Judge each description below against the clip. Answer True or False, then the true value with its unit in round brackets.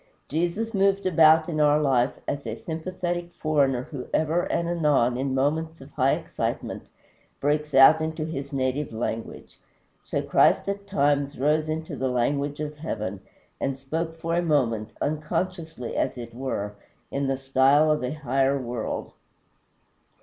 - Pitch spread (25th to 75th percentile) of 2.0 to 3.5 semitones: True (3.2 semitones)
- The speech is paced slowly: False (150 wpm)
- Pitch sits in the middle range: True (145 Hz)